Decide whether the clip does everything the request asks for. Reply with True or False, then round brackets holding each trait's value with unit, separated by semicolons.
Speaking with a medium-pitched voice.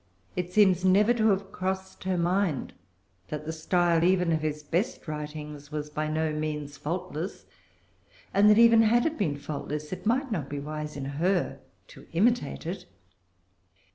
True (170 Hz)